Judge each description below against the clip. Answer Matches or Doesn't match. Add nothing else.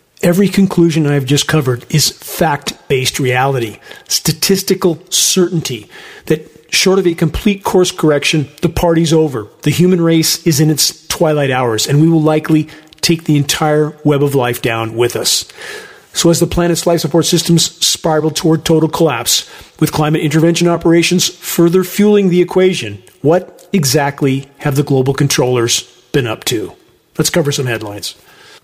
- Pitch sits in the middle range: Matches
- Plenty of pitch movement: Doesn't match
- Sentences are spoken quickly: Doesn't match